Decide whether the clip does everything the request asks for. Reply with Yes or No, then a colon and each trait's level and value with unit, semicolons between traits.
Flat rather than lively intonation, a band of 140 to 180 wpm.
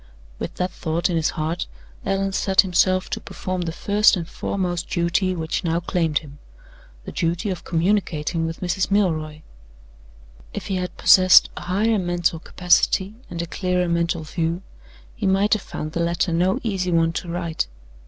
Yes: narrow, 2.2 semitones; average, 170 wpm